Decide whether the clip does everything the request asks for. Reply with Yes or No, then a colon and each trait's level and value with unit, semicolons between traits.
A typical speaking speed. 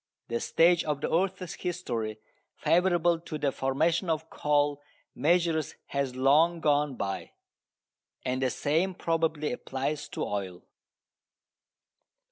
No: slow, 115 wpm